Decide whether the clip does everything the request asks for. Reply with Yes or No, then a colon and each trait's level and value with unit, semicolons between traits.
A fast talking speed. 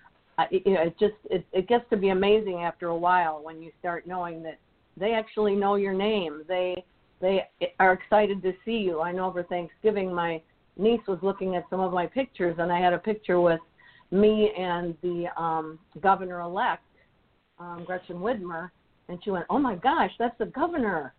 No: average, 180 wpm